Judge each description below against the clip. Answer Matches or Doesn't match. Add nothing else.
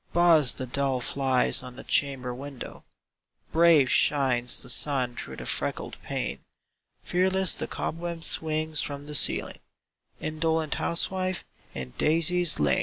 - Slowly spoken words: Matches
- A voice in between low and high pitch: Matches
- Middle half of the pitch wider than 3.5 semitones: Matches